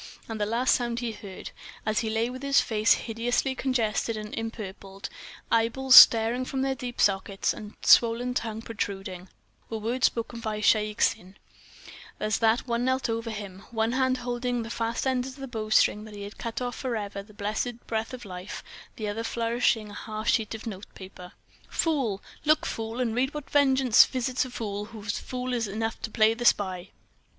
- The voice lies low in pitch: No, high, 225 Hz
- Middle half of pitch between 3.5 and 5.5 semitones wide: No, average, 2.7 semitones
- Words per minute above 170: Yes, average, 180 wpm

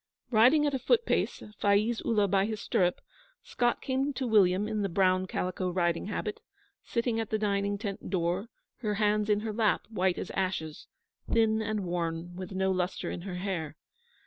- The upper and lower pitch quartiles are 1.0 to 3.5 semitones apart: Yes, average, 3.1 semitones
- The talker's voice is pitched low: No, high, 200 Hz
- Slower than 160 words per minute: No, average, 180 wpm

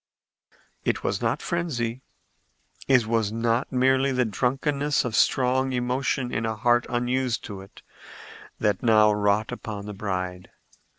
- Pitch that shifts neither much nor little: Yes, average, 3.4 semitones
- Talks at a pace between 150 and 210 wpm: No, slow, 135 wpm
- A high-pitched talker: No, low, 120 Hz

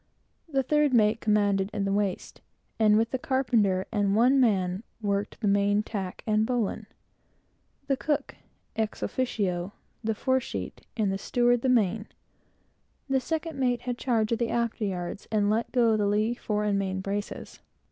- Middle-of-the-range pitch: No, high, 215 Hz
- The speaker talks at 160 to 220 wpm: Yes, average, 165 wpm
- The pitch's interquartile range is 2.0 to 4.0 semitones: Yes, average, 3.3 semitones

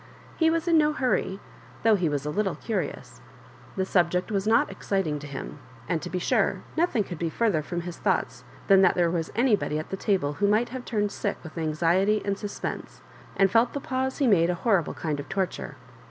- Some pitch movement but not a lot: Yes, average, 4.8 semitones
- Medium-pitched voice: No, high, 195 Hz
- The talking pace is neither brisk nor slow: No, fast, 210 wpm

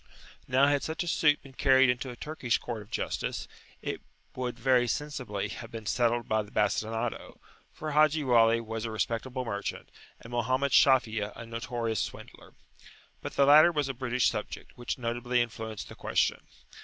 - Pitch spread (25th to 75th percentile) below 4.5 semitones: Yes, average, 2.9 semitones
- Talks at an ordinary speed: Yes, average, 170 wpm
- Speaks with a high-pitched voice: No, low, 120 Hz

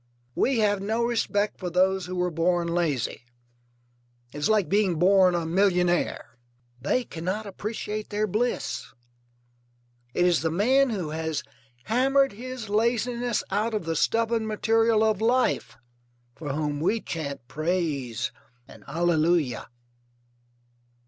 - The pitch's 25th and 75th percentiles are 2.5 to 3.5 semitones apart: No, average, 5.0 semitones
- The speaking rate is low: Yes, slow, 130 wpm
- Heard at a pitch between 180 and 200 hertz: Yes, high, 190 Hz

